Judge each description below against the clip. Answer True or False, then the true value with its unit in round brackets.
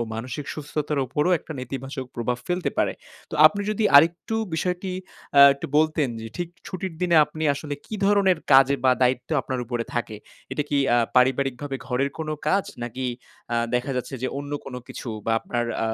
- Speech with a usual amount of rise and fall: True (4.2 semitones)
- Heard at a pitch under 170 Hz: True (140 Hz)